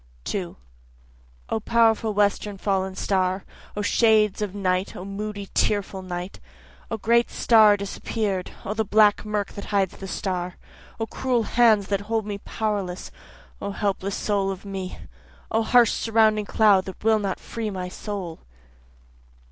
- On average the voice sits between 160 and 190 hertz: No, high, 205 Hz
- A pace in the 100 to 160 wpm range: Yes, average, 150 wpm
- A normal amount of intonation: No, narrow, 2.2 semitones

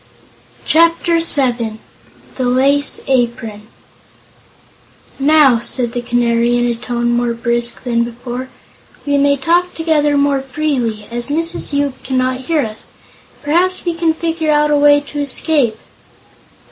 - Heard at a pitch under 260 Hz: No, very high, 265 Hz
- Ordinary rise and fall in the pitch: Yes, average, 3.9 semitones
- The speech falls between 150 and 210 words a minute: No, slow, 135 wpm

